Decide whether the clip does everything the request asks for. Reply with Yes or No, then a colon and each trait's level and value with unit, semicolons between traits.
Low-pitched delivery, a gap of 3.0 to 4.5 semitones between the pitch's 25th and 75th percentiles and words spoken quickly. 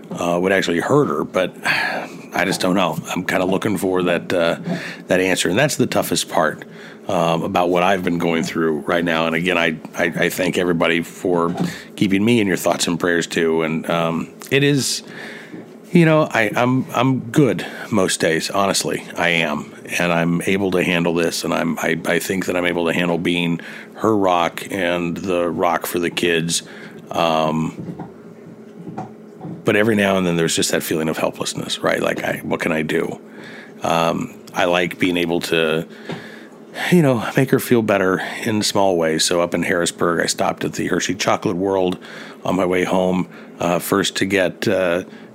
No: very low, 90 Hz; average, 3.6 semitones; average, 190 wpm